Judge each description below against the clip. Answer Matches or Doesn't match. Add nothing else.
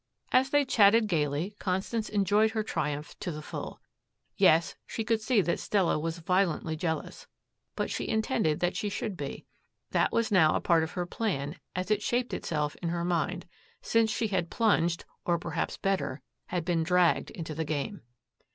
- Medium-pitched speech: Matches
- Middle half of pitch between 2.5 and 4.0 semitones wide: Doesn't match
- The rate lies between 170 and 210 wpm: Matches